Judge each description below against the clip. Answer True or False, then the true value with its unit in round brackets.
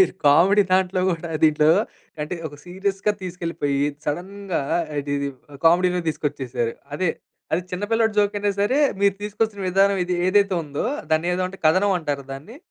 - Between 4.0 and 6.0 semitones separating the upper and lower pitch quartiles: True (4.4 semitones)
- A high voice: False (180 Hz)